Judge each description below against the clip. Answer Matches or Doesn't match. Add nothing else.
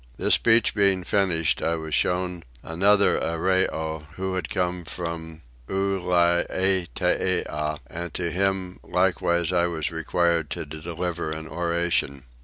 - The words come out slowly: Matches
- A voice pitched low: Matches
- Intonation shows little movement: Matches